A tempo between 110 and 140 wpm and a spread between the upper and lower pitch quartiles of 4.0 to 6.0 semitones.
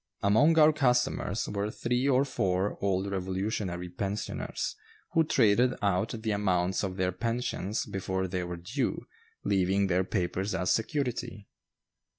Yes: slow, 135 wpm; average, 4.4 semitones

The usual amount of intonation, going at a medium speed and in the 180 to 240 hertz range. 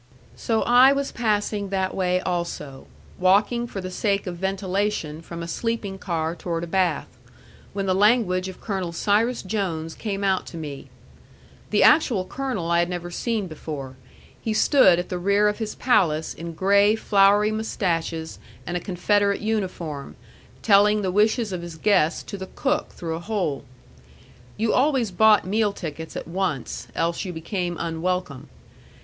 Yes: average, 3.6 semitones; average, 160 wpm; high, 190 Hz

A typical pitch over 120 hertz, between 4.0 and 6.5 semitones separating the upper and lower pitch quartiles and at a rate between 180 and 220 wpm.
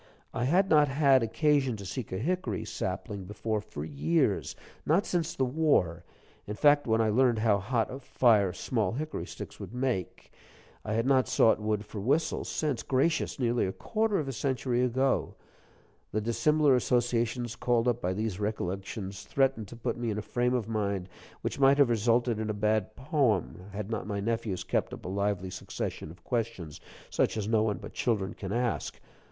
No: low, 115 Hz; average, 4.3 semitones; average, 185 wpm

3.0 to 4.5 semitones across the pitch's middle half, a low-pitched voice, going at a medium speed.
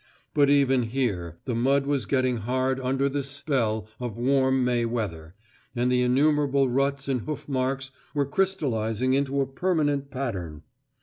No: narrow, 2.5 semitones; low, 130 Hz; average, 150 wpm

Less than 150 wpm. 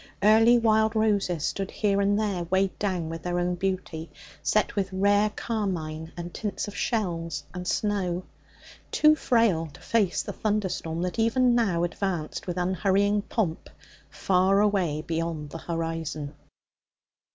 Yes: average, 140 wpm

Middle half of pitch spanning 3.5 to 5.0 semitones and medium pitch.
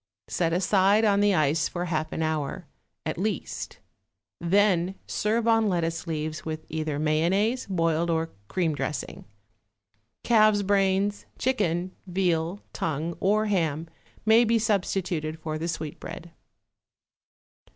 Yes: average, 4.2 semitones; medium, 175 Hz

